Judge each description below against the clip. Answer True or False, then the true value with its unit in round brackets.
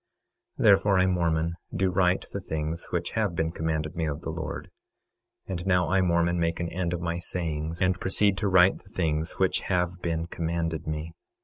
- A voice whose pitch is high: False (85 Hz)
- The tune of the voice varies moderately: False (2.2 semitones)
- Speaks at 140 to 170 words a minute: False (195 wpm)